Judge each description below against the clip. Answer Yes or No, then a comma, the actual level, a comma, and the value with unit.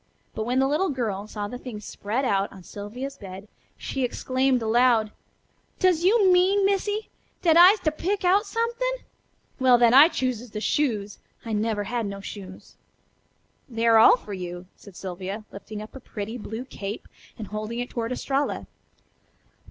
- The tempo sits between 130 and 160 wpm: No, average, 170 wpm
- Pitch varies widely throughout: Yes, wide, 5.9 semitones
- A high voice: Yes, high, 240 Hz